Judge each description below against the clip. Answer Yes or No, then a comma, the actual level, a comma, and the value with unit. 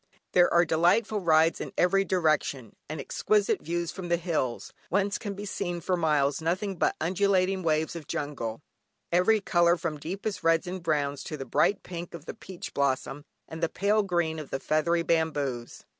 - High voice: No, medium, 170 Hz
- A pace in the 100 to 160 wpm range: No, average, 180 wpm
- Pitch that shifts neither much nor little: Yes, average, 3.3 semitones